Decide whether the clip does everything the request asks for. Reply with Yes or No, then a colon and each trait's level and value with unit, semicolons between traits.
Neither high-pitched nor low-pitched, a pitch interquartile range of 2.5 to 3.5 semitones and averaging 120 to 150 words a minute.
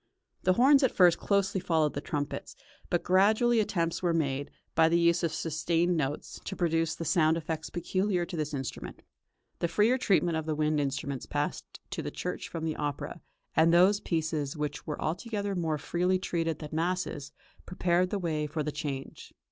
No: medium, 165 Hz; average, 3.0 semitones; average, 180 wpm